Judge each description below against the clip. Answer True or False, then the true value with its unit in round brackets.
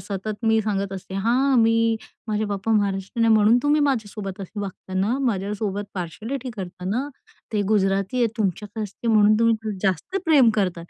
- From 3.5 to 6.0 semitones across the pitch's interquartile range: False (2.7 semitones)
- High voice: True (210 Hz)